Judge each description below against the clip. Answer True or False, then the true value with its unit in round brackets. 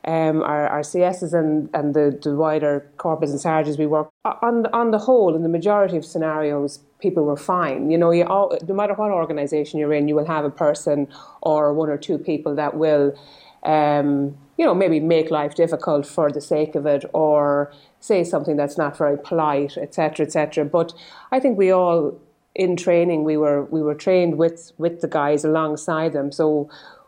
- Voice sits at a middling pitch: True (155 Hz)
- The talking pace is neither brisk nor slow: True (195 wpm)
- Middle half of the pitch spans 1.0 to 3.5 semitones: True (2.4 semitones)